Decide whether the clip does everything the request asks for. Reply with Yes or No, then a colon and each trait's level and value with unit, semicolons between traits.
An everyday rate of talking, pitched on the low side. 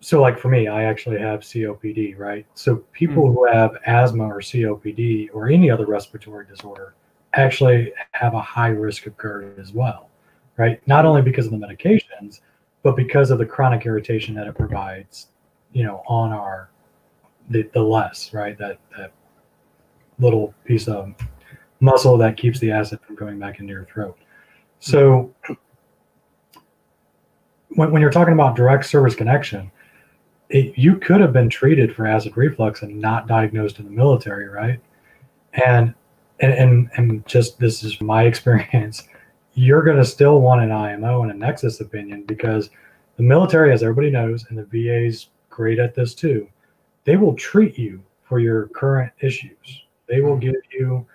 Yes: average, 165 wpm; low, 115 Hz